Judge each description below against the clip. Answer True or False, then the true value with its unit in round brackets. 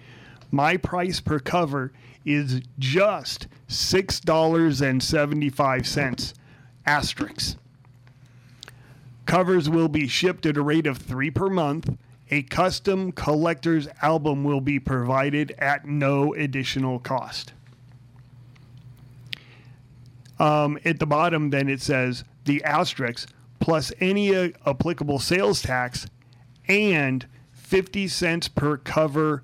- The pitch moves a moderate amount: True (3.7 semitones)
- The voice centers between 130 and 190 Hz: True (140 Hz)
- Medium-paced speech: False (100 wpm)